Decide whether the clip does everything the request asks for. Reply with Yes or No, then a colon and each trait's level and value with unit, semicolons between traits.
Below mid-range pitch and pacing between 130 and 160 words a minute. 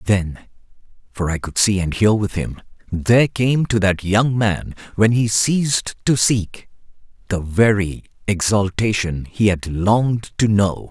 Yes: low, 105 Hz; average, 145 wpm